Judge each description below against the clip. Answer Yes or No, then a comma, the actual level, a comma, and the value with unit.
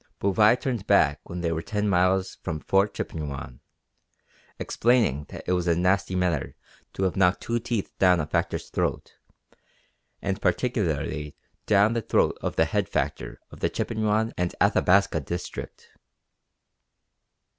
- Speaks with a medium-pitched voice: No, very low, 95 Hz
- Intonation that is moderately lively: Yes, average, 3.9 semitones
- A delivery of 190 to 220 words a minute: No, average, 145 wpm